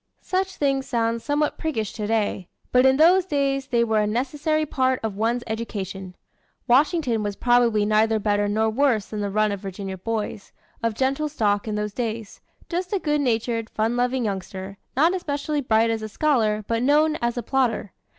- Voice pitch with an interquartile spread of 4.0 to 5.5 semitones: Yes, average, 4.5 semitones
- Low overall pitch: No, high, 230 Hz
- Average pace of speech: Yes, average, 180 wpm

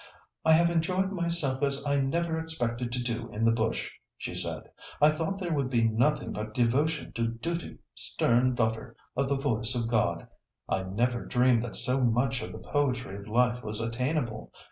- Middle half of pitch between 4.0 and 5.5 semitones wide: Yes, average, 4.5 semitones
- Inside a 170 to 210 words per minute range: Yes, average, 185 wpm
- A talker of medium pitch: No, low, 125 Hz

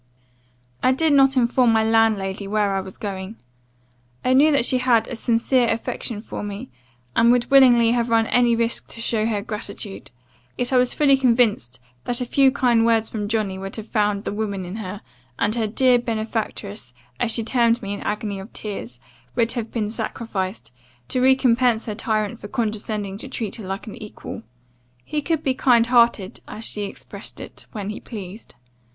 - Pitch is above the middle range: Yes, high, 225 Hz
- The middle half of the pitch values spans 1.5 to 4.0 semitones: Yes, average, 2.9 semitones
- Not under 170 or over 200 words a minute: Yes, average, 190 wpm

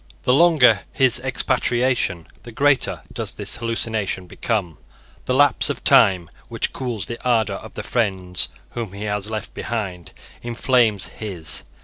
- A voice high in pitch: No, low, 110 Hz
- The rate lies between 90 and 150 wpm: Yes, average, 140 wpm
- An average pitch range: Yes, average, 4.1 semitones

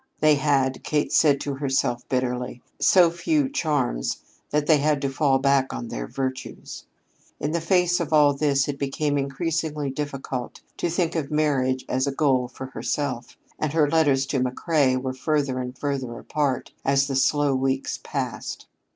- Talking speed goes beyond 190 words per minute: No, average, 170 wpm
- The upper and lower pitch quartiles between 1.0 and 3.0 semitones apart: Yes, narrow, 2.5 semitones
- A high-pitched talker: No, medium, 140 Hz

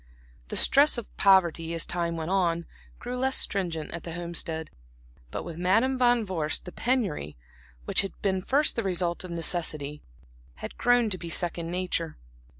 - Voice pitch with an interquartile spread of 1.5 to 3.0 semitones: No, average, 3.8 semitones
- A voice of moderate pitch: Yes, medium, 175 Hz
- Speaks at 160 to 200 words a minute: Yes, average, 165 wpm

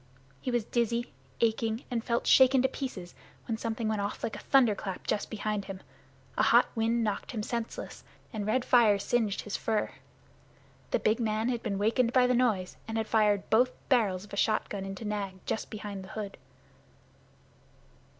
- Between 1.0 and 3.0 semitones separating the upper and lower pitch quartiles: Yes, narrow, 2.6 semitones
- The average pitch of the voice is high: Yes, high, 220 Hz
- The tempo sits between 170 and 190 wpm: Yes, average, 180 wpm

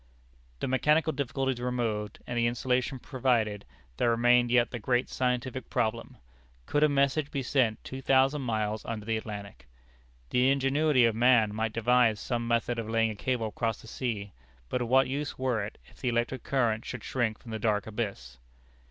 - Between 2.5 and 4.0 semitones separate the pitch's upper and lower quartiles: Yes, average, 2.9 semitones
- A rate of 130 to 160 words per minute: No, average, 180 wpm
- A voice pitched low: Yes, low, 120 Hz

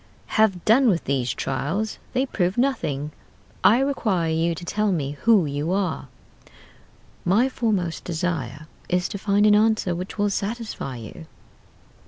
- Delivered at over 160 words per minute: No, average, 145 wpm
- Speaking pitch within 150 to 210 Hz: Yes, medium, 185 Hz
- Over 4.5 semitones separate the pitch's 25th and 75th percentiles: Yes, average, 5.3 semitones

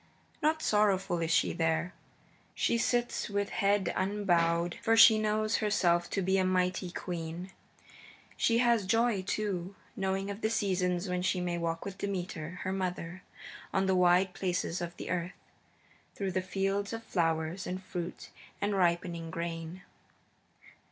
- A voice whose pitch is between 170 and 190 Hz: Yes, medium, 185 Hz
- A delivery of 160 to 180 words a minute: No, average, 145 wpm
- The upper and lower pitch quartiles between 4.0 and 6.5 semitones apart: No, narrow, 2.6 semitones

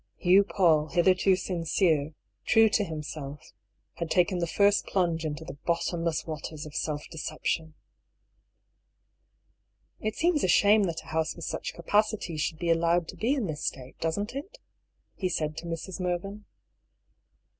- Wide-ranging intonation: No, average, 3.7 semitones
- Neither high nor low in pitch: Yes, medium, 170 Hz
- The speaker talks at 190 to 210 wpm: No, average, 165 wpm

